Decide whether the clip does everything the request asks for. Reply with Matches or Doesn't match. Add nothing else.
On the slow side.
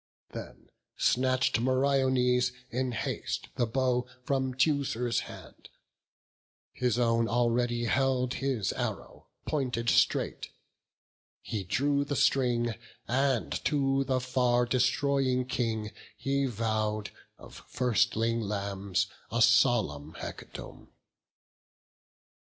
Matches